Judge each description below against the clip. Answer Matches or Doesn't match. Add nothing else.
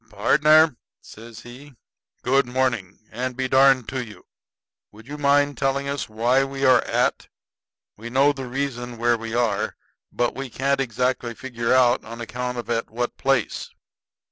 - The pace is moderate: Matches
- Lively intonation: Doesn't match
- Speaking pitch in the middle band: Doesn't match